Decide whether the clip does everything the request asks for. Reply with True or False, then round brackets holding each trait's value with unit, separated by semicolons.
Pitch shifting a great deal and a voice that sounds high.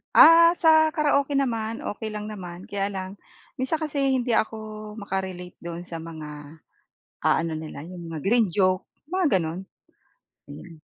True (7.1 semitones; 205 Hz)